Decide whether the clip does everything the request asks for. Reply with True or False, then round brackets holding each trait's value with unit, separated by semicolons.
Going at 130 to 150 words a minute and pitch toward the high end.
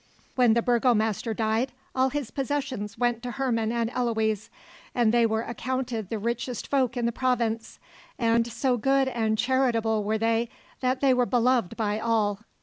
False (165 wpm; 235 Hz)